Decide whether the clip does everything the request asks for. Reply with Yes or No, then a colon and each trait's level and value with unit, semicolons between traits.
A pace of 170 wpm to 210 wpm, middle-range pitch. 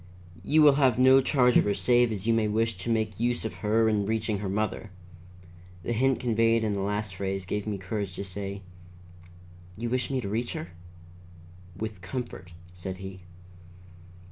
No: average, 180 wpm; low, 110 Hz